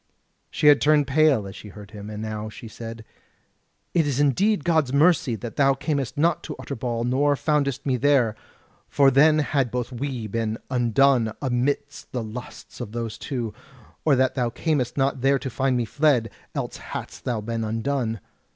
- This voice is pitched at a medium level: No, low, 130 Hz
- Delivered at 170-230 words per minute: Yes, average, 180 wpm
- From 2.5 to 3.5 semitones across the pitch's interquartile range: No, average, 3.9 semitones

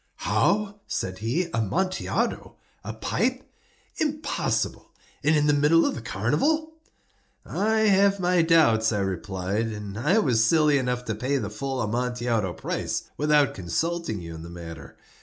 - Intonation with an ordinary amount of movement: No, wide, 8.1 semitones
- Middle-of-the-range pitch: No, low, 125 Hz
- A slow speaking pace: No, average, 145 wpm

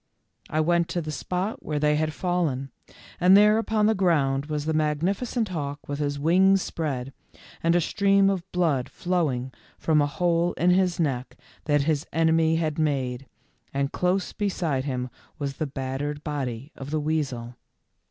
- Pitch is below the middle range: No, medium, 155 Hz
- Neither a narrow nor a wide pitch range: Yes, average, 4.0 semitones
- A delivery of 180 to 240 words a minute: No, average, 170 wpm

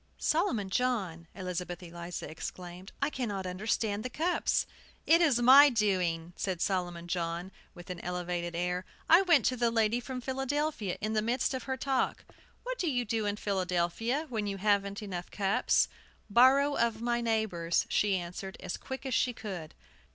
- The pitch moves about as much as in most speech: No, wide, 5.9 semitones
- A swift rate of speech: No, average, 165 wpm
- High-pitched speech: Yes, high, 210 Hz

